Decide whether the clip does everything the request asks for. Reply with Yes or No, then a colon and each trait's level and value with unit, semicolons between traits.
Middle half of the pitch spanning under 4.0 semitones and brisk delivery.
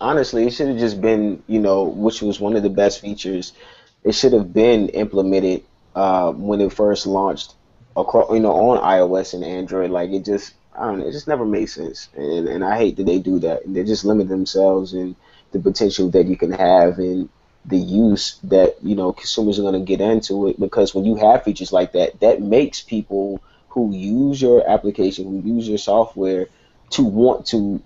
Yes: narrow, 2.5 semitones; fast, 210 wpm